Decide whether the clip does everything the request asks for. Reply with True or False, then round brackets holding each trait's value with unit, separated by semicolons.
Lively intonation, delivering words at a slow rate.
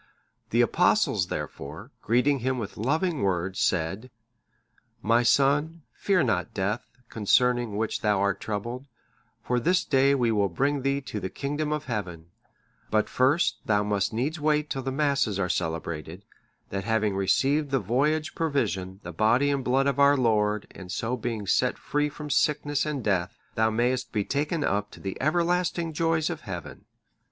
False (5.8 semitones; 165 wpm)